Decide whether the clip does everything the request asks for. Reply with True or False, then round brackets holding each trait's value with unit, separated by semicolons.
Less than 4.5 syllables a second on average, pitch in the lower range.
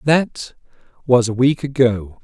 True (3.9 syllables/s; 130 Hz)